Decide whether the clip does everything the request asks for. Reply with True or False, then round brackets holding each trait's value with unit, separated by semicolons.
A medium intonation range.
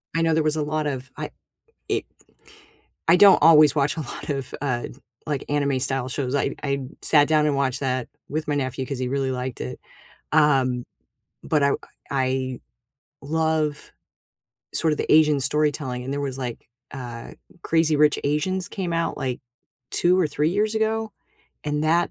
True (3.0 semitones)